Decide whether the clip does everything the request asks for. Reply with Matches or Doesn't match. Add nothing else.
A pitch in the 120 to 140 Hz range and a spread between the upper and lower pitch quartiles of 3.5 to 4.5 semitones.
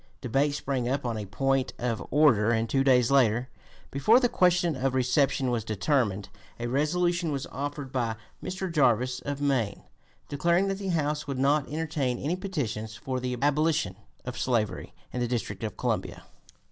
Matches